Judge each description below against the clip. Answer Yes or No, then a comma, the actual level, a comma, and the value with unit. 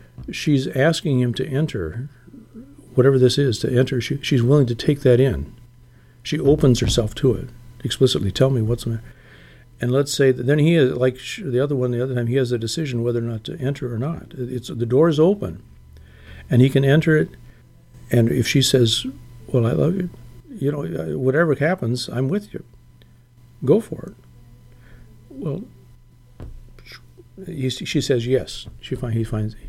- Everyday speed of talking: Yes, average, 180 wpm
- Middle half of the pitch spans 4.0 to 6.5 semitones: No, narrow, 2.5 semitones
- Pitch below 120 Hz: No, low, 125 Hz